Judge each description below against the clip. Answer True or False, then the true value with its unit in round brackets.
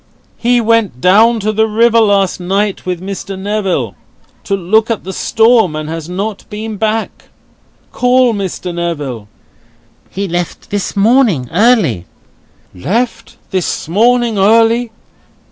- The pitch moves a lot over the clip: False (4.0 semitones)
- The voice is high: True (205 Hz)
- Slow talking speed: True (130 wpm)